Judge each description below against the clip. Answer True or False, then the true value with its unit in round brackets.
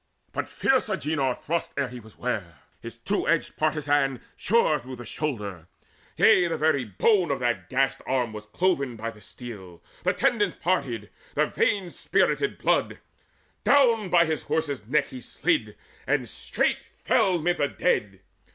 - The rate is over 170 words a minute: False (160 wpm)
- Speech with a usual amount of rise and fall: False (6.5 semitones)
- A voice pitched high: False (140 Hz)